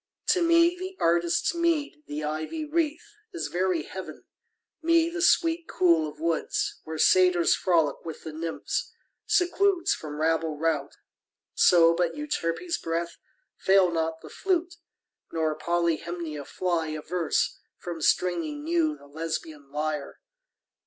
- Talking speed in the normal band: No, slow, 130 wpm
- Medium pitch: Yes, medium, 170 Hz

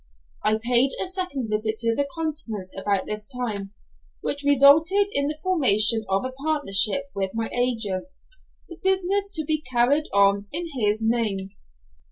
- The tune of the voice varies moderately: No, wide, 6.3 semitones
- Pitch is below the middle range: No, high, 245 Hz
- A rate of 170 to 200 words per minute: No, average, 155 wpm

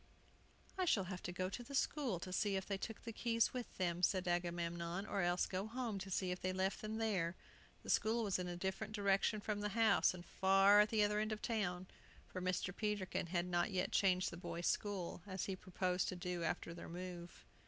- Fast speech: Yes, fast, 225 wpm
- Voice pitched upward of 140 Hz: Yes, high, 190 Hz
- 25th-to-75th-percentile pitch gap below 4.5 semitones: Yes, average, 2.8 semitones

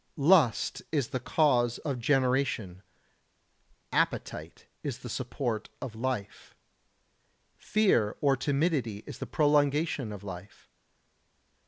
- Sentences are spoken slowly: Yes, slow, 110 wpm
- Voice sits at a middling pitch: No, low, 130 Hz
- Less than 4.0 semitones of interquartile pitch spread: No, average, 4.5 semitones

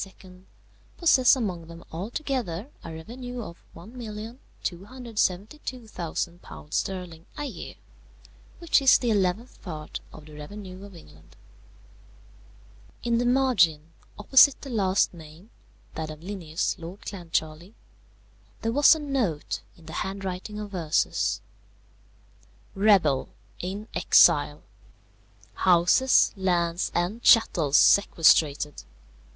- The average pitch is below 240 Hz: Yes, high, 190 Hz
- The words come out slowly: Yes, slow, 100 wpm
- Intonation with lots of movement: Yes, wide, 5.8 semitones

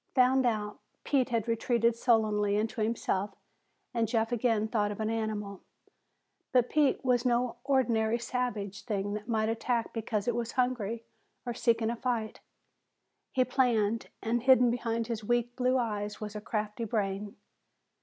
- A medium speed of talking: Yes, average, 155 wpm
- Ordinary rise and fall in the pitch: No, narrow, 2.3 semitones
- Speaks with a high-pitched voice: Yes, high, 230 Hz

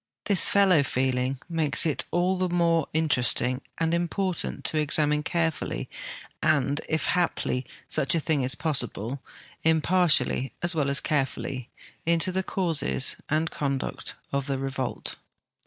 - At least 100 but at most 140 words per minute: Yes, slow, 135 wpm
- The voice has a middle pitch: Yes, medium, 155 Hz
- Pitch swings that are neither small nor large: Yes, average, 3.9 semitones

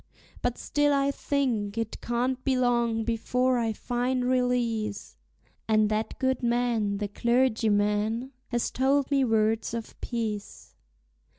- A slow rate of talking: Yes, slow, 125 wpm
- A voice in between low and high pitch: No, high, 235 Hz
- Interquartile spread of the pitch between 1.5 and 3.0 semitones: Yes, average, 2.7 semitones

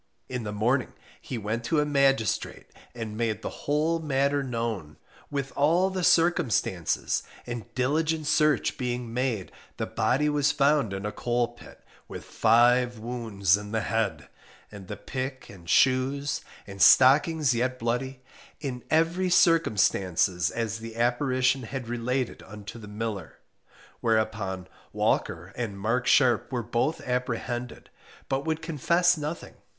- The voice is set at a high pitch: No, low, 125 Hz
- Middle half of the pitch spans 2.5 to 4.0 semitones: No, average, 4.4 semitones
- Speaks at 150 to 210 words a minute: No, average, 140 wpm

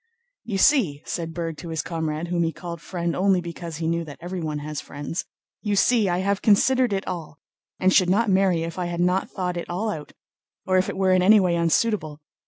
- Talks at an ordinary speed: No, fast, 220 wpm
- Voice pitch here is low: No, medium, 175 Hz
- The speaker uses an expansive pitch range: No, average, 2.8 semitones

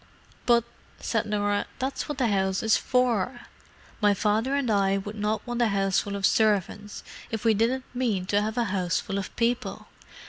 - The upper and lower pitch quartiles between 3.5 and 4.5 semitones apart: No, average, 3.1 semitones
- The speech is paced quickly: No, average, 175 wpm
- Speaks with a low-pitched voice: No, high, 215 Hz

